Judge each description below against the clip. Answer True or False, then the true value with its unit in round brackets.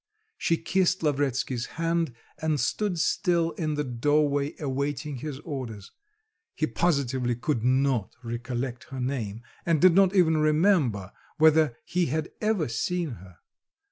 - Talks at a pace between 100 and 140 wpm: True (135 wpm)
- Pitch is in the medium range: True (145 Hz)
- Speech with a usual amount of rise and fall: True (4.9 semitones)